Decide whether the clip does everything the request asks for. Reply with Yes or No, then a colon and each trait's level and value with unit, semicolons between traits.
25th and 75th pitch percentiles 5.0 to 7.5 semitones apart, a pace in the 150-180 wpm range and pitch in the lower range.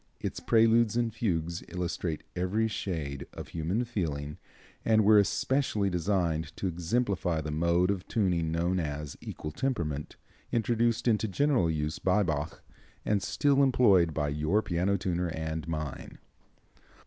No: wide, 5.4 semitones; slow, 135 wpm; very low, 90 Hz